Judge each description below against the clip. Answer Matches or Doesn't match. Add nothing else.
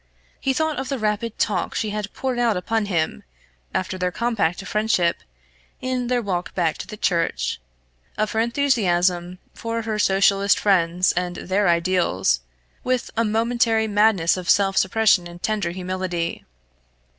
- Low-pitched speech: Doesn't match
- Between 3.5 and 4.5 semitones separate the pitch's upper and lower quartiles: Matches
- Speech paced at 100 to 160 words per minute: Matches